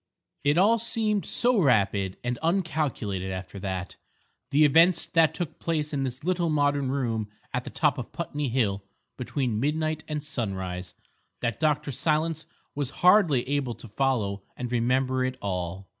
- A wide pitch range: Yes, wide, 5.9 semitones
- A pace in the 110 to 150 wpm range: Yes, average, 145 wpm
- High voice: No, low, 135 Hz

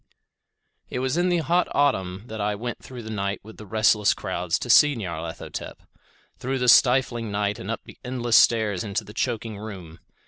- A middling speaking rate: Yes, average, 185 wpm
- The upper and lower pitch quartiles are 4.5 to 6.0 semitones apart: No, average, 3.7 semitones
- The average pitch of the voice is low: Yes, low, 110 Hz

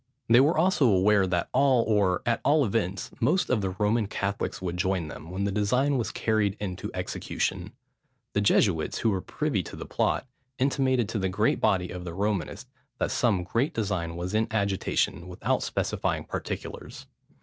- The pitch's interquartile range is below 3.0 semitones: No, average, 4.1 semitones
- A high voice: No, low, 100 Hz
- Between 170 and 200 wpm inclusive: Yes, average, 175 wpm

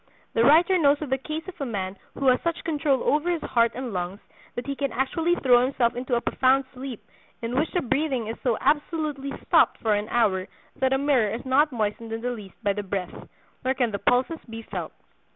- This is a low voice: No, very high, 255 Hz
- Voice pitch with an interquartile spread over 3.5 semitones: Yes, average, 4.1 semitones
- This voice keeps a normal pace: No, fast, 225 wpm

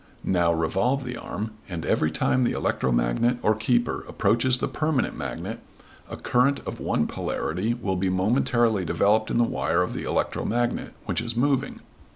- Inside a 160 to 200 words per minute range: Yes, average, 165 wpm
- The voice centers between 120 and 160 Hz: No, low, 110 Hz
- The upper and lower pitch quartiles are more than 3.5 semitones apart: Yes, wide, 5.5 semitones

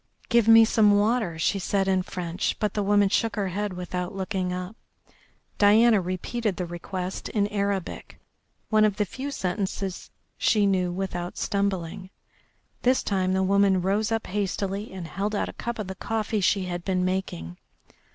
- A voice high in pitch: Yes, high, 195 Hz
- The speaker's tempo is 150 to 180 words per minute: Yes, average, 170 wpm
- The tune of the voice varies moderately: No, narrow, 2.3 semitones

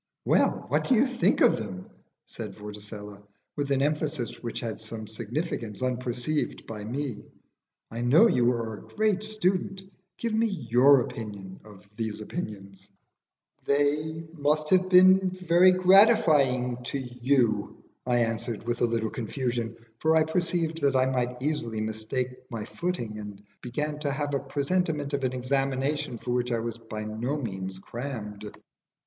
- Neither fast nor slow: Yes, average, 155 wpm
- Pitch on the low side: Yes, low, 125 Hz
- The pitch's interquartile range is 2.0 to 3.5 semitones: No, wide, 5.4 semitones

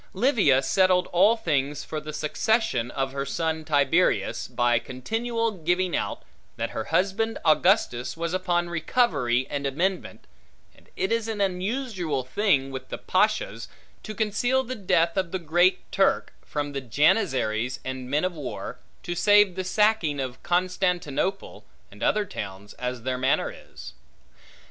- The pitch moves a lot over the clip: Yes, wide, 6.6 semitones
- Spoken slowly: No, average, 150 wpm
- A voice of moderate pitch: Yes, medium, 170 Hz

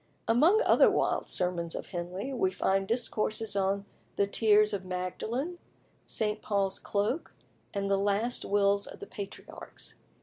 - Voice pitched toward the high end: Yes, high, 200 Hz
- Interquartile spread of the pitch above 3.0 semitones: No, narrow, 2.5 semitones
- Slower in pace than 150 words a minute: Yes, average, 140 wpm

